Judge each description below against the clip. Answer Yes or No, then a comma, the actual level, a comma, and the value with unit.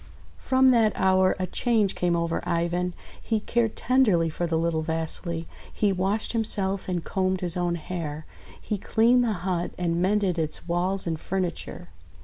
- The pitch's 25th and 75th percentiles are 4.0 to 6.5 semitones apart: No, average, 3.4 semitones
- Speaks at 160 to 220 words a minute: Yes, average, 170 wpm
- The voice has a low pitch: No, medium, 185 Hz